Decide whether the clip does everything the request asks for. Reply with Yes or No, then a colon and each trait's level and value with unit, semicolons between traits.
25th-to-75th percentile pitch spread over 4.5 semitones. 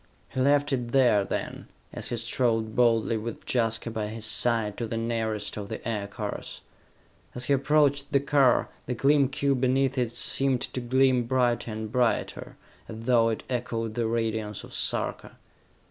No: narrow, 2.6 semitones